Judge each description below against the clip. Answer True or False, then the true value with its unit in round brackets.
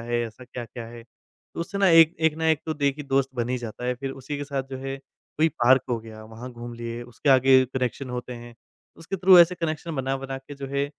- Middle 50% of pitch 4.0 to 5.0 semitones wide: False (3.6 semitones)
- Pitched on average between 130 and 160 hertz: True (135 Hz)